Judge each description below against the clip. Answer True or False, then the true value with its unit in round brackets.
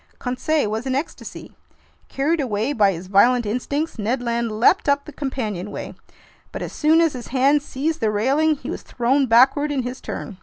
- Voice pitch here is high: True (255 Hz)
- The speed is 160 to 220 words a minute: True (185 wpm)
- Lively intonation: False (4.3 semitones)